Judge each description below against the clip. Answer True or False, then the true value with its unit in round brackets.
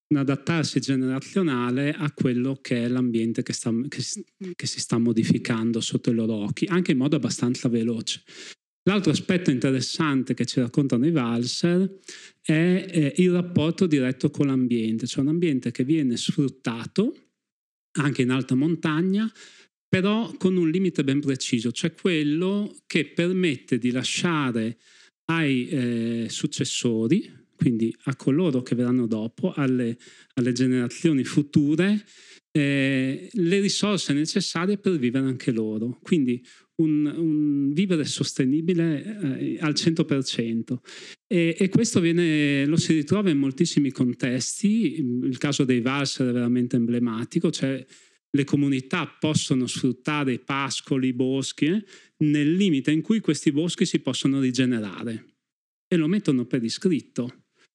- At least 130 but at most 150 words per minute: True (135 wpm)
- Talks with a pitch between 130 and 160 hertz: True (140 Hz)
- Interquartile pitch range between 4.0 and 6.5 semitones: True (4.9 semitones)